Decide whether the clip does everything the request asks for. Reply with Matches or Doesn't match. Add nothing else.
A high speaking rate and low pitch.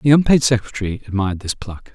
Doesn't match